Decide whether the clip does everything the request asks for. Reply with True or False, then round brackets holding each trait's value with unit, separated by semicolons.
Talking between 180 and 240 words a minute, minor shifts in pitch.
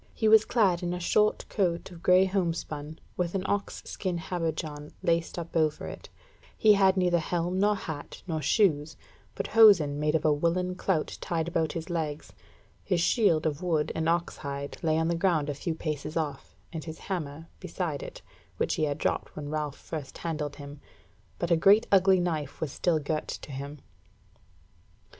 False (185 wpm; 3.2 semitones)